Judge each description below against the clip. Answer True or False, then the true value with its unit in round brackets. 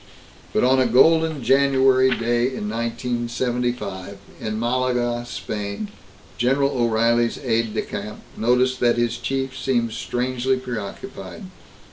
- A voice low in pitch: True (120 Hz)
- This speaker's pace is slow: True (115 wpm)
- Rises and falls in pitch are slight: True (2.0 semitones)